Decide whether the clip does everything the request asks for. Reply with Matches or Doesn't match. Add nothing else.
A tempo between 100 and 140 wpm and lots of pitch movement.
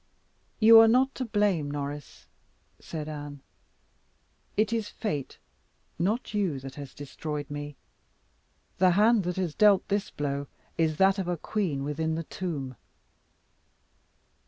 Matches